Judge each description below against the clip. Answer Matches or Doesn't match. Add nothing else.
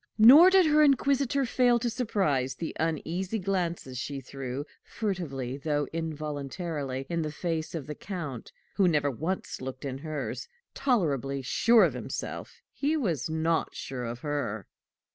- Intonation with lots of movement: Matches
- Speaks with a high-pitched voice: Doesn't match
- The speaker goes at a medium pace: Matches